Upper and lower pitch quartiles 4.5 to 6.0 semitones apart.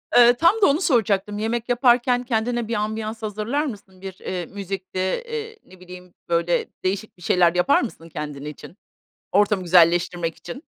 Yes: average, 5.0 semitones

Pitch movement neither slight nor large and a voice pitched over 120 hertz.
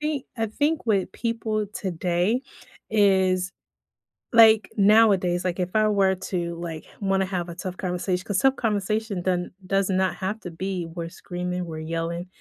Yes: average, 3.1 semitones; high, 190 Hz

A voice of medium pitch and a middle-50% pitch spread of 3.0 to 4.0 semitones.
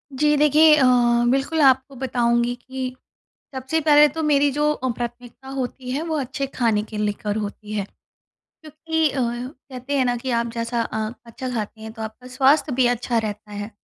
No: very high, 255 Hz; average, 3.3 semitones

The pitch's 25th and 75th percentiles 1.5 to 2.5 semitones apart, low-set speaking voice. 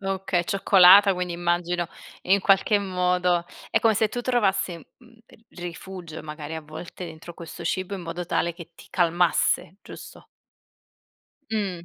No: narrow, 2.2 semitones; medium, 180 Hz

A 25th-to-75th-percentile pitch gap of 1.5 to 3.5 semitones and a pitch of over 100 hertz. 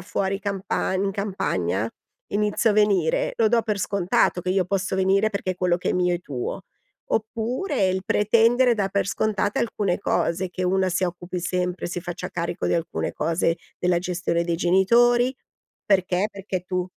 Yes: narrow, 2.5 semitones; high, 190 Hz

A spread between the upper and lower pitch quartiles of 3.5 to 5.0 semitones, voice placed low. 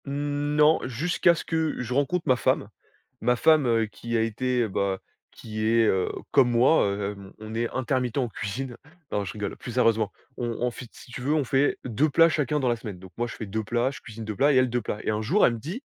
Yes: average, 4.2 semitones; low, 120 Hz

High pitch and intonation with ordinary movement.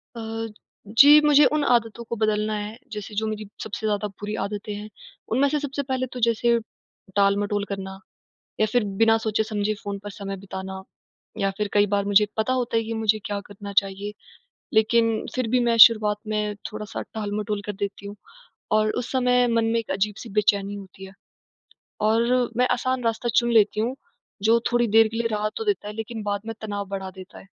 No: high, 215 Hz; narrow, 2.2 semitones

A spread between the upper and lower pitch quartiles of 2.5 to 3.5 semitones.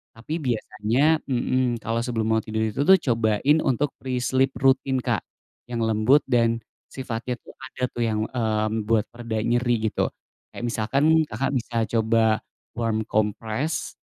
Yes: average, 2.9 semitones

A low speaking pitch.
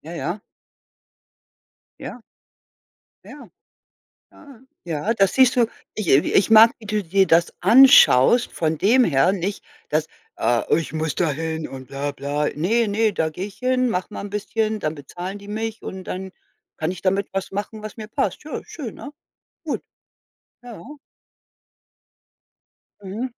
No: high, 195 Hz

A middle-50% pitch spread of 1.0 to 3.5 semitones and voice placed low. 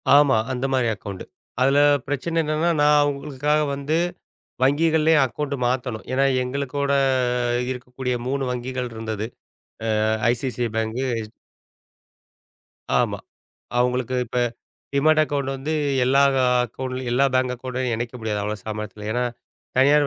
Yes: average, 2.8 semitones; low, 130 Hz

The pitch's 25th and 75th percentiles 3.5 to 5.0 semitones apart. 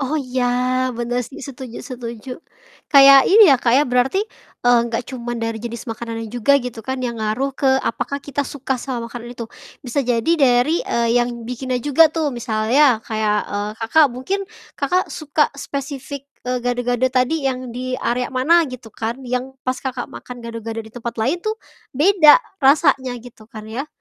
No: average, 2.8 semitones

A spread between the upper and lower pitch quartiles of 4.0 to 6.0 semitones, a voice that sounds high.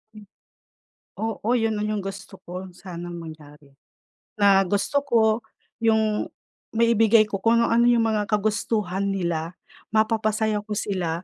No: average, 3.1 semitones; high, 210 Hz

